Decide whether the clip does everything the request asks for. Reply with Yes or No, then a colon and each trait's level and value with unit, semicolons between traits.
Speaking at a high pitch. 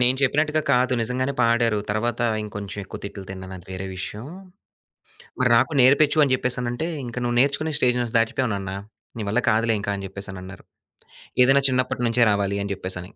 No: low, 120 Hz